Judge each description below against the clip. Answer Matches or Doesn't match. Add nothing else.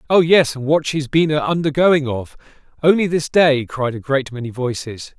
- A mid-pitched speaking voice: Matches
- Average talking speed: Matches